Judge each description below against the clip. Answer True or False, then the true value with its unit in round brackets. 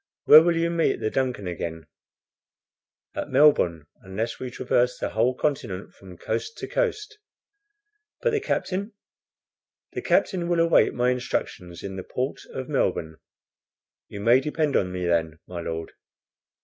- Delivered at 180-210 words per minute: False (150 wpm)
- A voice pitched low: True (125 Hz)